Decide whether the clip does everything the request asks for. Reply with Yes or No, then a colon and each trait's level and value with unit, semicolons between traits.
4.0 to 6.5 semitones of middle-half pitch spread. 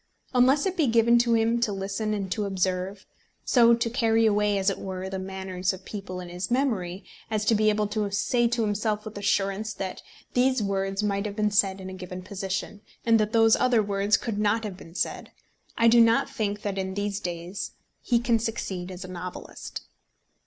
No: average, 3.0 semitones